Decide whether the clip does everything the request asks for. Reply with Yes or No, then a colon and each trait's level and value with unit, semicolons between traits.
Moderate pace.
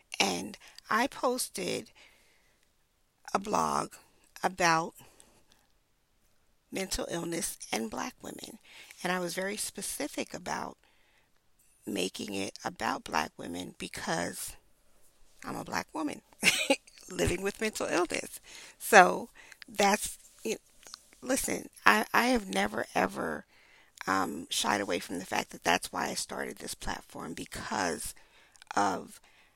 No: slow, 115 wpm